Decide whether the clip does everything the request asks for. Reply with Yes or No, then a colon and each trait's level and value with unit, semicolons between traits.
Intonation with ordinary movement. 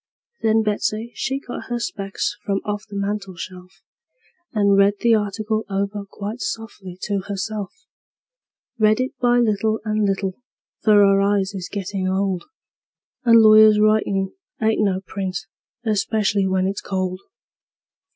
No: narrow, 1.8 semitones